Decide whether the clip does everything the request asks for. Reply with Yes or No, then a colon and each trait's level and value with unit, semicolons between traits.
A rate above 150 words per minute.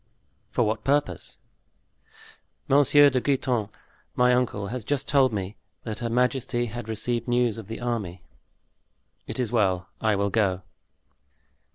No: average, 140 wpm